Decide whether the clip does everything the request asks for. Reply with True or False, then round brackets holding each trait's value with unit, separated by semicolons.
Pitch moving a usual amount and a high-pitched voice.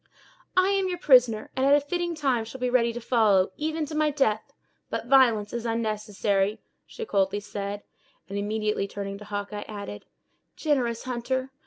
True (4.9 semitones; 230 Hz)